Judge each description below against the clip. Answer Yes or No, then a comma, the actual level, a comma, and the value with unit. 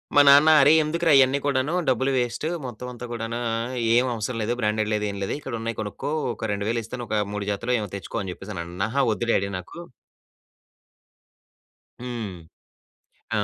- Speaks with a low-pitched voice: Yes, low, 115 Hz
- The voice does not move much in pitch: No, average, 3.7 semitones